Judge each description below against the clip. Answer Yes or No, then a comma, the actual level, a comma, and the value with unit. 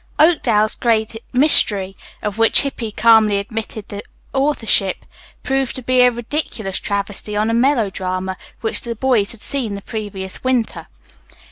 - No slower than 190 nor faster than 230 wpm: No, average, 140 wpm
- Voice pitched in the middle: No, high, 225 Hz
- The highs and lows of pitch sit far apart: No, average, 3.6 semitones